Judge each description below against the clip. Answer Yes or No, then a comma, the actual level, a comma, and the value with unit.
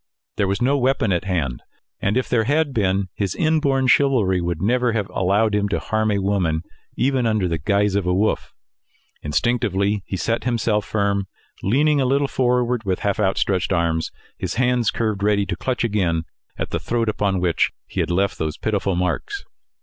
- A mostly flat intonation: No, average, 4.4 semitones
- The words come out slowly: No, average, 185 wpm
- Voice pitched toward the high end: No, low, 105 Hz